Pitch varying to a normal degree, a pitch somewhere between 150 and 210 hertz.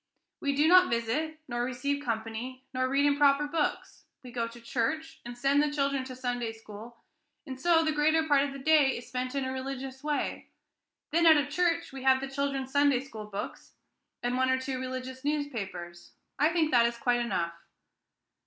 No: average, 3.1 semitones; very high, 265 Hz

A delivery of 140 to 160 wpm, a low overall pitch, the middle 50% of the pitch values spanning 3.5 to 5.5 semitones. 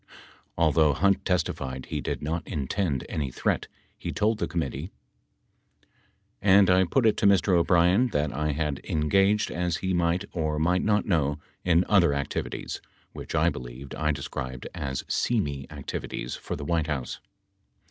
Yes: average, 155 wpm; very low, 80 Hz; average, 4.7 semitones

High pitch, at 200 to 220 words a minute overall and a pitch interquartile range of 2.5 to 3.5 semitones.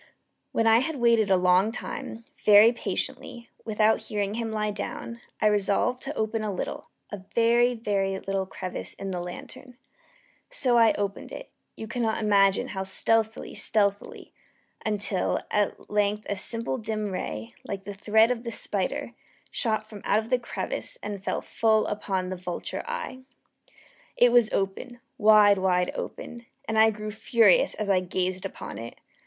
No: high, 215 Hz; average, 160 wpm; average, 2.8 semitones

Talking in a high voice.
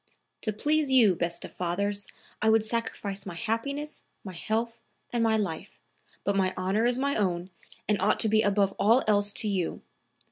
Yes: high, 210 Hz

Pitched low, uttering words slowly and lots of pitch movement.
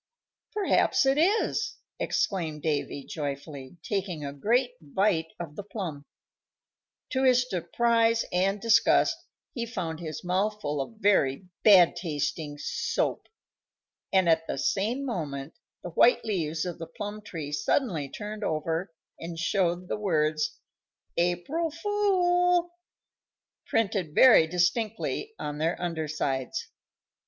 No: medium, 180 Hz; slow, 125 wpm; wide, 6.4 semitones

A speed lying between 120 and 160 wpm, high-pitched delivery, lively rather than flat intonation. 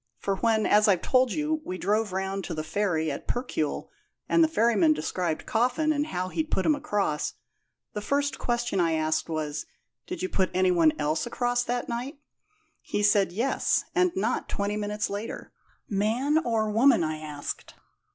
No: average, 175 wpm; high, 210 Hz; wide, 5.8 semitones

